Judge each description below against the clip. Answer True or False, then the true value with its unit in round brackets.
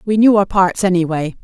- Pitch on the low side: False (190 Hz)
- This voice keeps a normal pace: False (210 wpm)